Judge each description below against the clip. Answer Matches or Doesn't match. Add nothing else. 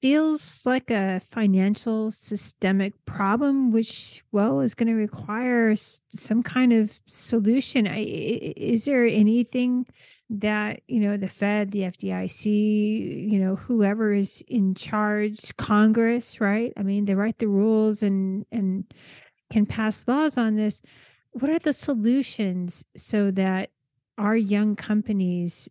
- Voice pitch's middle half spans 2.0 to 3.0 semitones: Matches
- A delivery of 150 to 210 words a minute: Doesn't match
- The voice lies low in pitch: Doesn't match